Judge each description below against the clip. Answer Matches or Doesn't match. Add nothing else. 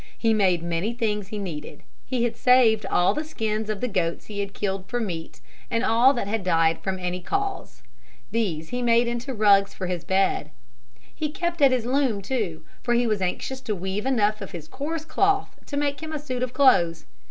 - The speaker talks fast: Matches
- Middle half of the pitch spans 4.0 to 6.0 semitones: Matches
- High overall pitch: Matches